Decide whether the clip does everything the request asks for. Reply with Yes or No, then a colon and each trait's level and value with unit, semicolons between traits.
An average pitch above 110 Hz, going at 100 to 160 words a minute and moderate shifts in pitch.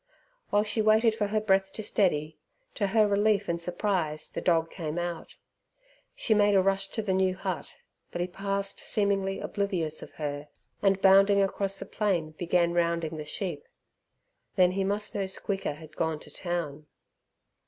No: high, 190 Hz; average, 170 wpm; average, 3.2 semitones